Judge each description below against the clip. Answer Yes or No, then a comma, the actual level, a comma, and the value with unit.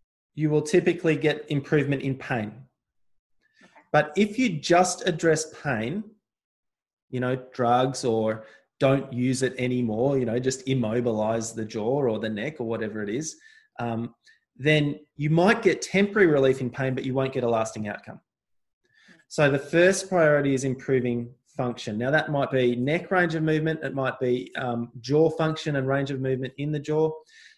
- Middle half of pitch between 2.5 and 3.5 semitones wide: No, average, 4.2 semitones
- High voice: No, low, 135 Hz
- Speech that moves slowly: No, average, 170 wpm